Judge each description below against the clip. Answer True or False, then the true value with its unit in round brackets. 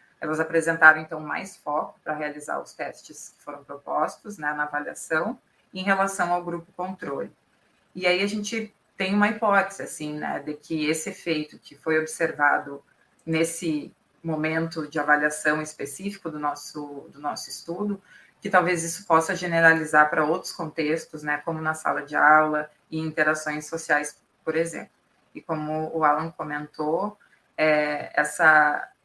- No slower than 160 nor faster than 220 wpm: False (150 wpm)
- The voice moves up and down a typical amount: False (2.3 semitones)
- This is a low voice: False (160 Hz)